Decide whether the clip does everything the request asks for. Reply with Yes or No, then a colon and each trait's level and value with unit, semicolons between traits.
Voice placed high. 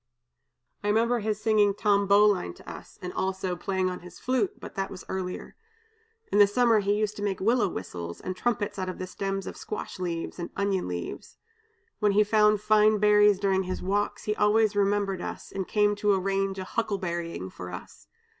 Yes: high, 200 Hz